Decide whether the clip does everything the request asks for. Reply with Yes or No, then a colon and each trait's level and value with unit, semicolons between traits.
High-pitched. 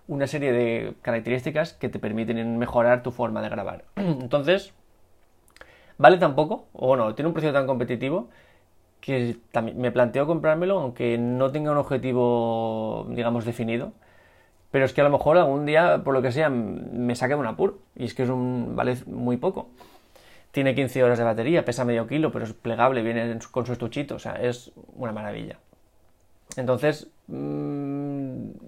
No: low, 125 Hz